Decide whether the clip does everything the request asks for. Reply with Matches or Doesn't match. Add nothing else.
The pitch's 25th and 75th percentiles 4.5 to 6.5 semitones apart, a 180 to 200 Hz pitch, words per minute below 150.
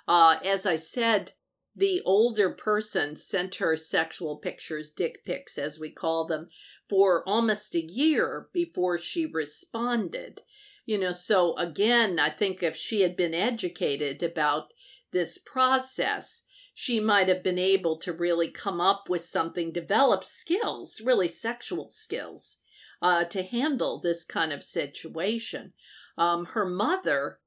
Matches